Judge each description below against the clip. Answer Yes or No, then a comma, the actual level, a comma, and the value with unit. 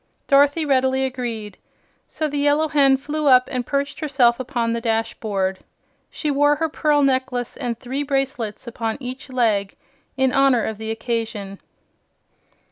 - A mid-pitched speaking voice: No, very high, 260 Hz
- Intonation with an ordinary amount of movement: Yes, average, 3.6 semitones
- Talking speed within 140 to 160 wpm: Yes, average, 145 wpm